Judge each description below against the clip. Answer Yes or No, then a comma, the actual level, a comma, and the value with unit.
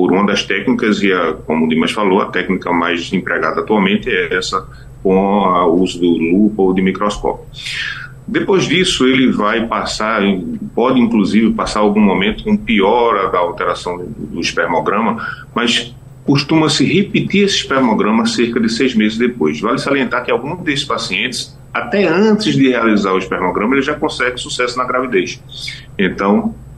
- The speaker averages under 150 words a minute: No, average, 160 wpm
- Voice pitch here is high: No, low, 125 Hz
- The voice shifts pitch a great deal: Yes, wide, 6.6 semitones